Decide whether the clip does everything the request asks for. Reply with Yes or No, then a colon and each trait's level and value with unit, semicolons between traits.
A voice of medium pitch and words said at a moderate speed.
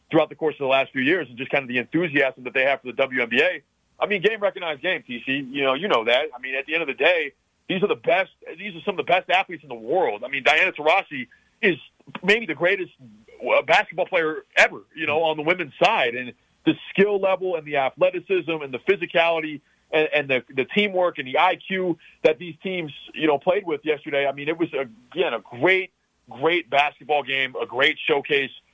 No: medium, 160 Hz; fast, 230 wpm